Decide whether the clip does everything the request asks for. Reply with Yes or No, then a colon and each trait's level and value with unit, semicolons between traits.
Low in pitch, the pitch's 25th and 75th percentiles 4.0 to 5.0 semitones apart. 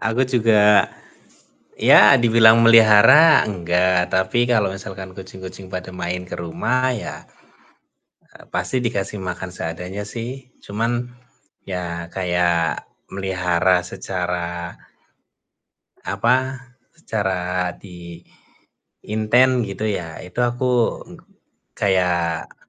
Yes: very low, 95 Hz; average, 4.4 semitones